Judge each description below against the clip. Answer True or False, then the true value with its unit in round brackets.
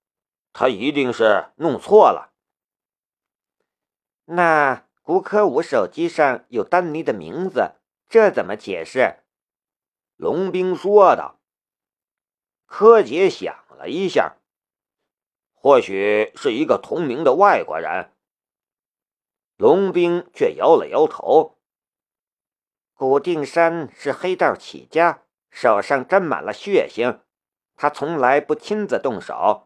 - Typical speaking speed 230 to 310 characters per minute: False (155 characters per minute)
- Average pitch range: False (6.7 semitones)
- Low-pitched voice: False (185 Hz)